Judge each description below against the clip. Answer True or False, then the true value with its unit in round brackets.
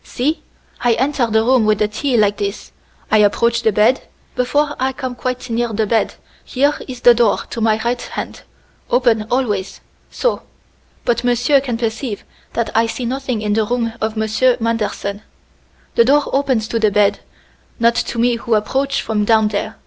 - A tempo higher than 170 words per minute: True (180 wpm)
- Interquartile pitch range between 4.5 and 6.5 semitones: False (2.7 semitones)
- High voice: True (235 Hz)